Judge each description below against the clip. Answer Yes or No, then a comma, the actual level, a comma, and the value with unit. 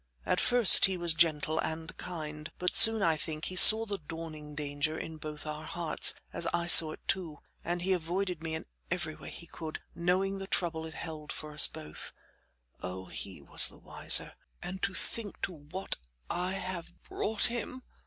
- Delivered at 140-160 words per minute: No, average, 185 wpm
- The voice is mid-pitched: Yes, medium, 165 Hz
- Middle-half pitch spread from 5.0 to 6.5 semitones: No, average, 3.3 semitones